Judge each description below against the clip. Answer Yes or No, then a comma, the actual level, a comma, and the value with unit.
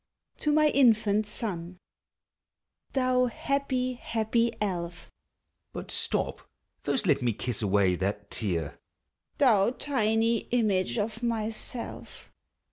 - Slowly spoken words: Yes, slow, 105 wpm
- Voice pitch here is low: No, high, 220 Hz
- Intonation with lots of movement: Yes, wide, 6.2 semitones